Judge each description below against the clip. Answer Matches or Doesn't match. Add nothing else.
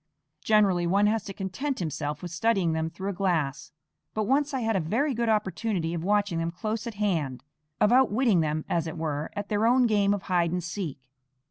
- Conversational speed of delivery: Doesn't match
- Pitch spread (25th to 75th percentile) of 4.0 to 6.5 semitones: Matches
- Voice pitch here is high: Matches